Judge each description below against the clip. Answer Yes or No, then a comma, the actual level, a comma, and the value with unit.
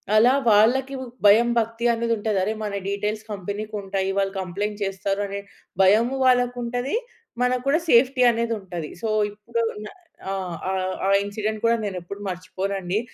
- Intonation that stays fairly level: No, average, 3.1 semitones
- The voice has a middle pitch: No, high, 210 Hz